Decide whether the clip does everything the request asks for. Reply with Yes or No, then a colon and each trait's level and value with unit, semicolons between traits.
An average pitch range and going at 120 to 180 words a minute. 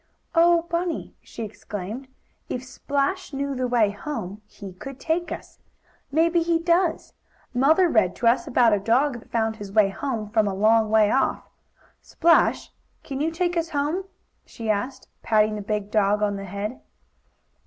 No: wide, 7.1 semitones; average, 165 wpm